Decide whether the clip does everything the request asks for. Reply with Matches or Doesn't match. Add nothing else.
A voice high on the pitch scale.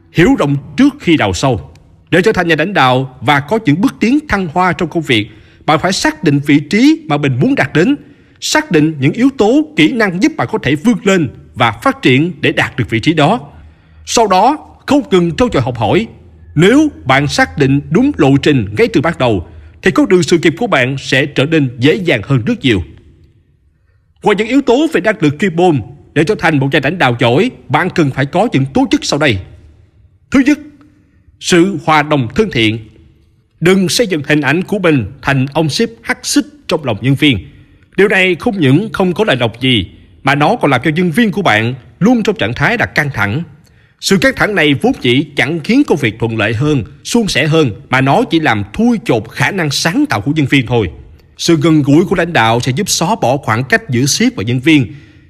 Doesn't match